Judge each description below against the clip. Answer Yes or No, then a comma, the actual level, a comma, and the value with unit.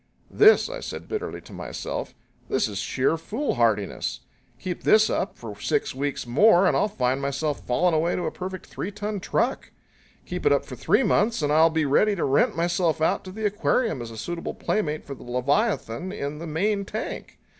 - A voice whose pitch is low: No, medium, 165 Hz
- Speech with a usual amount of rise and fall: No, wide, 7.1 semitones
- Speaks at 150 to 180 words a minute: No, average, 195 wpm